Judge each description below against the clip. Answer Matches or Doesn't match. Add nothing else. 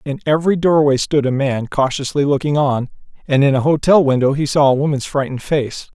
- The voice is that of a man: Matches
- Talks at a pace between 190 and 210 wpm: Matches